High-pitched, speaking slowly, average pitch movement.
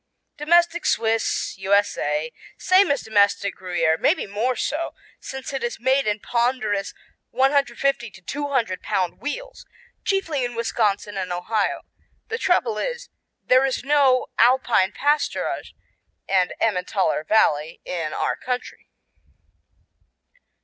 No: high, 235 Hz; slow, 115 wpm; wide, 6.0 semitones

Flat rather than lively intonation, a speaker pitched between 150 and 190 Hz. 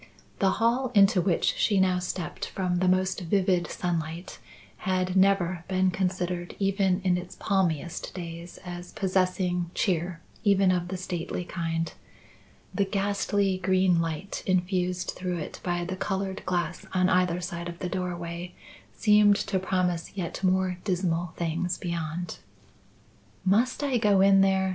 Yes: narrow, 1.6 semitones; medium, 185 Hz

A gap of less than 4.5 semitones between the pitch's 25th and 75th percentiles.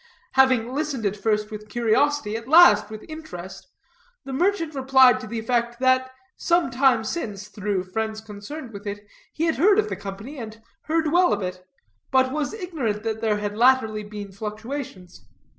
No: average, 5.0 semitones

